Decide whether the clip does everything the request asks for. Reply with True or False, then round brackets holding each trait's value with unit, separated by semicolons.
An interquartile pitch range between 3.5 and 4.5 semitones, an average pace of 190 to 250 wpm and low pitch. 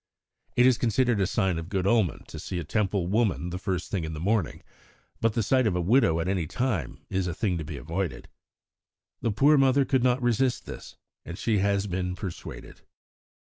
False (5.1 semitones; 205 wpm; 100 Hz)